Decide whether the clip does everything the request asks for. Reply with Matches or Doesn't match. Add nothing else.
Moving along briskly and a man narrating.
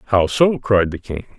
Matches